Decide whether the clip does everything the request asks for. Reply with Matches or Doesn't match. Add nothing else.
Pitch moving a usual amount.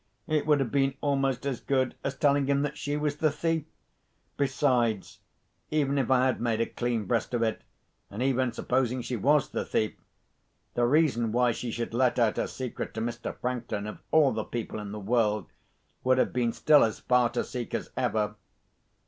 Matches